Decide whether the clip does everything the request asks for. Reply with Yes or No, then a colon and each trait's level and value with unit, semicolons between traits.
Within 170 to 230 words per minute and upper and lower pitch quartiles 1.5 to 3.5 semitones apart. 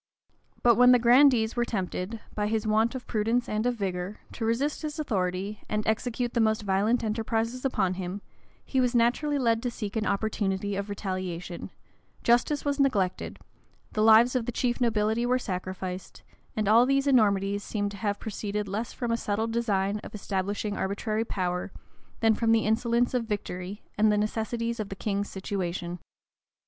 Yes: average, 175 wpm; average, 3.0 semitones